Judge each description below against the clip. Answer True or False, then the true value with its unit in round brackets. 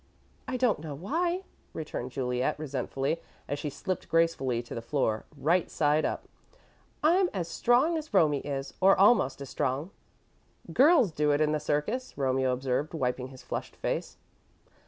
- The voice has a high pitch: False (150 Hz)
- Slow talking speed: False (155 wpm)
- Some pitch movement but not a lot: False (6.5 semitones)